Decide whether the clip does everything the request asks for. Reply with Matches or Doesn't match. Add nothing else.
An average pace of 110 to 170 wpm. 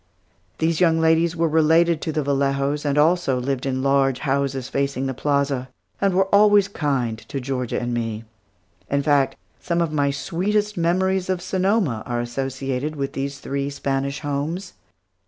Matches